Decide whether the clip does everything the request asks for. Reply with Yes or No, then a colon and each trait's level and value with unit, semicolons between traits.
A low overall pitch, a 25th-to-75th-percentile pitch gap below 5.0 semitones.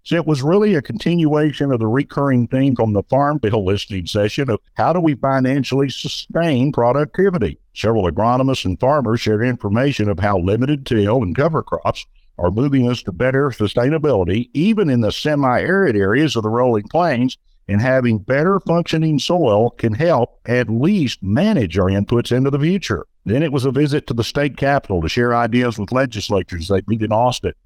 No: low, 125 Hz; average, 5.3 semitones